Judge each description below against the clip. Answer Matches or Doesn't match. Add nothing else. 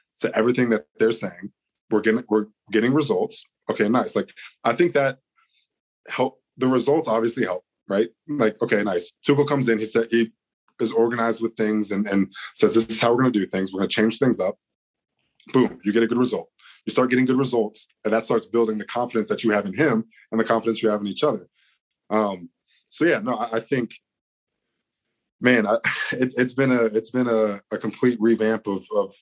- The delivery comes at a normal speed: Doesn't match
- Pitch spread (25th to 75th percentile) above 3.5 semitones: Doesn't match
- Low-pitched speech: Matches